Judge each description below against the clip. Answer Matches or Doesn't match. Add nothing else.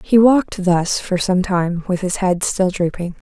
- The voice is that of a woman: Matches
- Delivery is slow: Doesn't match